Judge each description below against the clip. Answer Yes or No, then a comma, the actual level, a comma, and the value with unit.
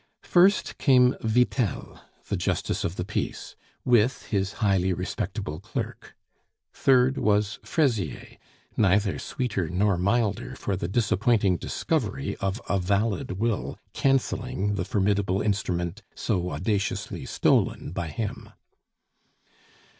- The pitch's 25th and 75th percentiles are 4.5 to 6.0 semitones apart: No, average, 3.9 semitones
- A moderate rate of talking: No, slow, 110 wpm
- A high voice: No, low, 100 Hz